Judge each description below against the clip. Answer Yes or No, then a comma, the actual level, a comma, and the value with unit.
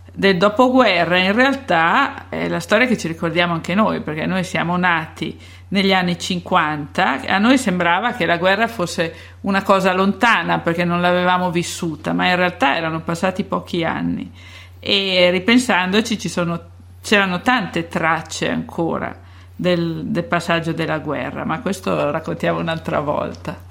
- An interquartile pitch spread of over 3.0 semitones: No, average, 2.7 semitones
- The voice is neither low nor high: Yes, medium, 180 Hz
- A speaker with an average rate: Yes, average, 150 wpm